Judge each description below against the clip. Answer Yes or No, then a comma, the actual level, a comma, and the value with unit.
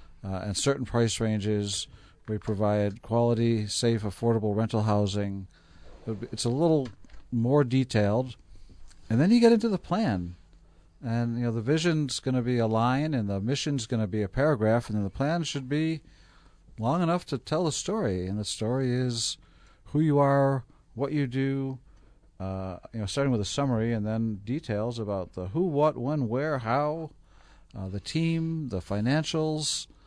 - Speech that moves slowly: No, average, 170 wpm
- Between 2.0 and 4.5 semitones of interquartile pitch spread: No, wide, 5.4 semitones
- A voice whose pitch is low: Yes, low, 115 Hz